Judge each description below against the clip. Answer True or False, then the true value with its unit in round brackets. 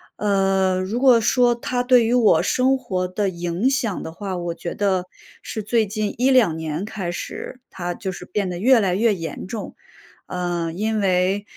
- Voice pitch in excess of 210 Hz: False (200 Hz)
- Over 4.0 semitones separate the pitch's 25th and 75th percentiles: True (4.4 semitones)